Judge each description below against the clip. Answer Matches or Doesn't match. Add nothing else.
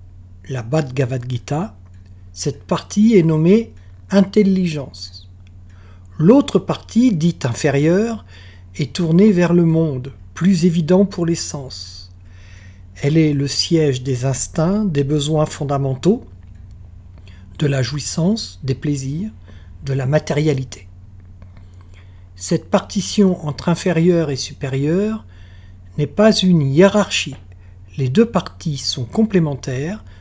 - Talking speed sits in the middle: Doesn't match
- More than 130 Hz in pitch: Matches